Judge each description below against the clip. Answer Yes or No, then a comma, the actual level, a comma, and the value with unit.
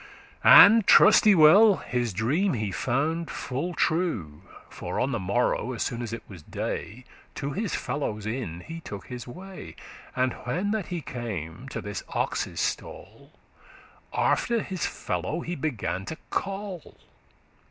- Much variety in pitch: Yes, wide, 8.1 semitones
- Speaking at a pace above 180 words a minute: No, average, 145 wpm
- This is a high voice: No, low, 135 Hz